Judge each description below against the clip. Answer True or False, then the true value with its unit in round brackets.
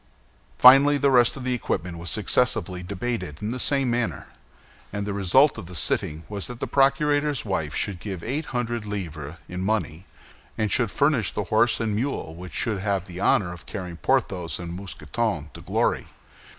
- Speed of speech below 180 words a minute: False (185 wpm)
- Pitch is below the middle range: True (105 Hz)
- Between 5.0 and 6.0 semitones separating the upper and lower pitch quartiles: True (5.6 semitones)